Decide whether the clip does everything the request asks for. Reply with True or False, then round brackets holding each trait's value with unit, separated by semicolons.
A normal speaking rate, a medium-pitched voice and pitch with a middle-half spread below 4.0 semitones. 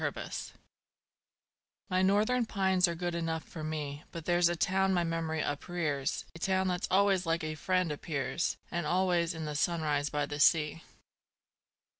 True (160 wpm; 170 Hz; 2.9 semitones)